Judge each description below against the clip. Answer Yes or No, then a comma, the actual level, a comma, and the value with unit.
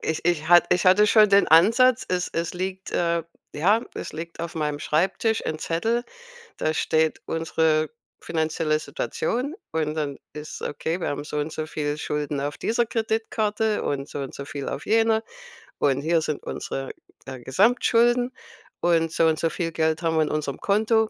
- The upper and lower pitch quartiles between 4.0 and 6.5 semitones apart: Yes, wide, 5.5 semitones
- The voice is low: No, medium, 165 Hz